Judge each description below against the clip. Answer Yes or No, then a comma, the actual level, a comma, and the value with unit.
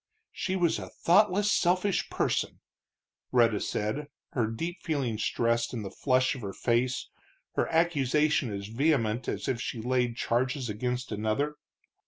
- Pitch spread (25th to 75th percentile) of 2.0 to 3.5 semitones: No, average, 4.8 semitones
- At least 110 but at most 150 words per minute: Yes, average, 145 wpm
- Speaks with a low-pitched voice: Yes, low, 125 Hz